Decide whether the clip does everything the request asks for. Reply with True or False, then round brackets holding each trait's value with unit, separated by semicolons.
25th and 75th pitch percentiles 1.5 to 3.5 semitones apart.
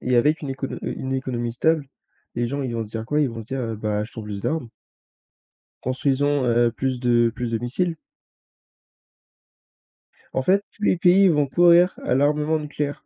False (4.1 semitones)